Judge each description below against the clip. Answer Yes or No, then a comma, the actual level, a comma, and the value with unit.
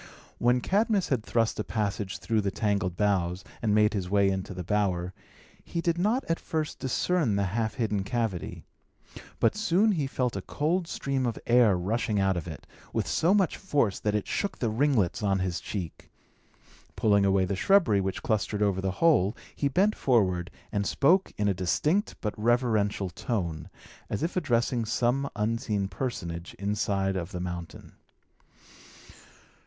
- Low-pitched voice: Yes, low, 105 Hz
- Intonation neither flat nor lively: No, wide, 5.7 semitones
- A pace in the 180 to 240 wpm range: No, average, 165 wpm